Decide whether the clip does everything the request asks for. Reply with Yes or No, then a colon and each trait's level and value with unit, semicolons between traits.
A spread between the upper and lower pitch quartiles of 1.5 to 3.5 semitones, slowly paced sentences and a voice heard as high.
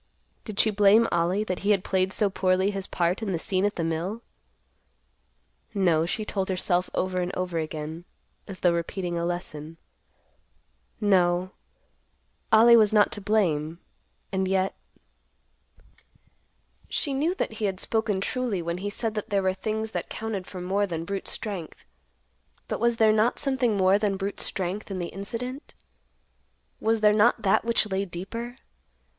No: average, 3.2 semitones; average, 160 wpm; high, 195 Hz